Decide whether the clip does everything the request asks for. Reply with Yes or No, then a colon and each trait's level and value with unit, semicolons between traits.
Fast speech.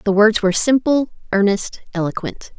No: average, 140 wpm